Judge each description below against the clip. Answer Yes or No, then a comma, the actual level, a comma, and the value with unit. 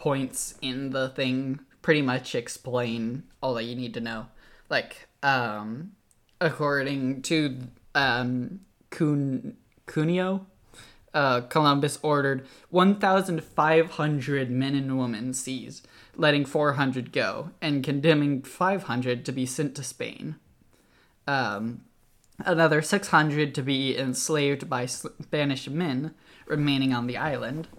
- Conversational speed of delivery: No, slow, 110 wpm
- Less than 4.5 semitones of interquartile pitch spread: Yes, average, 3.4 semitones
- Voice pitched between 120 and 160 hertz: Yes, medium, 140 Hz